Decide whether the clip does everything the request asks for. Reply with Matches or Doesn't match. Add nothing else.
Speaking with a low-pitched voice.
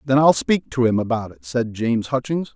Matches